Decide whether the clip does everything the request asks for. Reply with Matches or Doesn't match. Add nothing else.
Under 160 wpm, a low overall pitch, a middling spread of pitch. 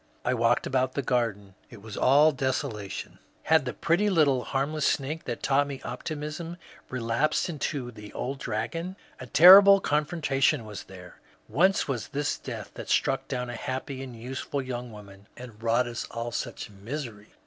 Doesn't match